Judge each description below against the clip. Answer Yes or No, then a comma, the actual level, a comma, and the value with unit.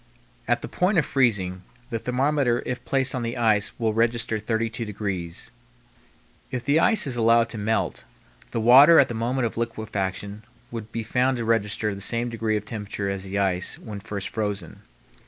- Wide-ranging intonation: No, average, 2.9 semitones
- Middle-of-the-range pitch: No, low, 115 Hz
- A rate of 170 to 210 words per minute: Yes, average, 180 wpm